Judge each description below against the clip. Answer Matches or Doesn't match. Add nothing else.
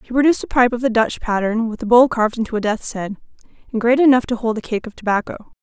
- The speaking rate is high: Matches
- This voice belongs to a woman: Matches